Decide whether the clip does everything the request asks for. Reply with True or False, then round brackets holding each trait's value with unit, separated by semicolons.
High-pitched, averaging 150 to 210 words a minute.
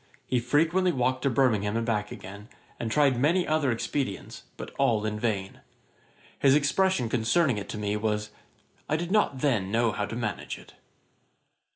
False (120 Hz; 170 wpm)